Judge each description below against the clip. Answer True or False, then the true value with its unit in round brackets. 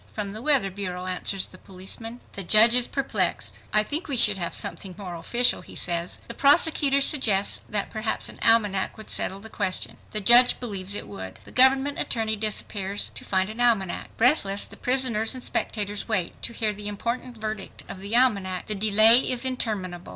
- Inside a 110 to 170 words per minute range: False (190 wpm)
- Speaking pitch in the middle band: False (215 Hz)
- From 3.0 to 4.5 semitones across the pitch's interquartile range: True (3.9 semitones)